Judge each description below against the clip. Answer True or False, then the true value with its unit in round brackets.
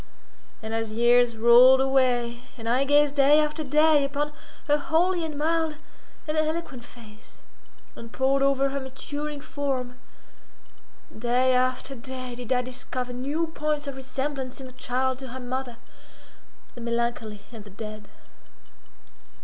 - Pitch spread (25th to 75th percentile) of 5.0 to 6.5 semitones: False (3.1 semitones)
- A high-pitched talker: True (260 Hz)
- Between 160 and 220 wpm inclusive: False (140 wpm)